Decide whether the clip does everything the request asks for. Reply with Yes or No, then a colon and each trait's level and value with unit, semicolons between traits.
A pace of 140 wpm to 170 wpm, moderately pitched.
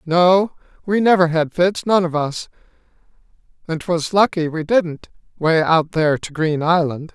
Yes: average, 160 wpm; medium, 170 Hz